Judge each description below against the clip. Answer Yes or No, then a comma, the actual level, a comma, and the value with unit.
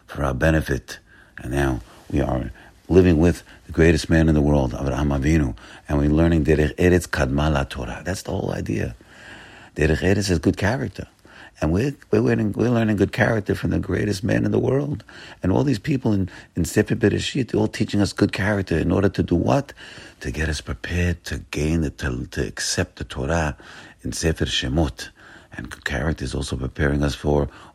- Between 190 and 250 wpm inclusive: Yes, average, 195 wpm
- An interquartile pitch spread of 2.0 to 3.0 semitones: No, wide, 5.4 semitones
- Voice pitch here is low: Yes, very low, 85 Hz